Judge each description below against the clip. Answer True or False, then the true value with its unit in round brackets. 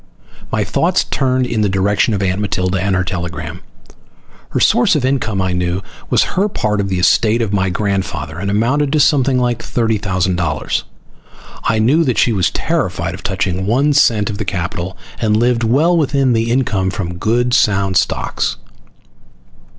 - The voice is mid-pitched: False (105 Hz)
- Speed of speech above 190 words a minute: False (175 wpm)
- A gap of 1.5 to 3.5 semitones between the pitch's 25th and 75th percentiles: False (4.8 semitones)